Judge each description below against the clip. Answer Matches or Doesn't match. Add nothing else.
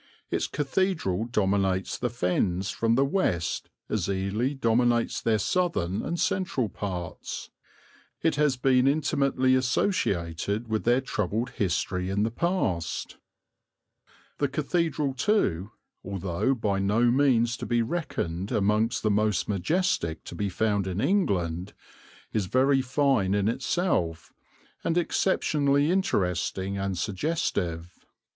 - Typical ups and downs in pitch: Doesn't match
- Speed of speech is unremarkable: Doesn't match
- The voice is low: Matches